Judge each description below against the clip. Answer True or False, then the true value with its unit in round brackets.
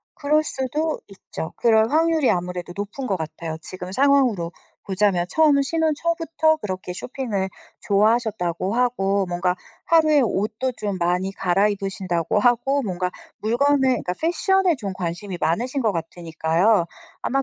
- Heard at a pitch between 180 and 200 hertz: False (210 Hz)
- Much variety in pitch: True (7.3 semitones)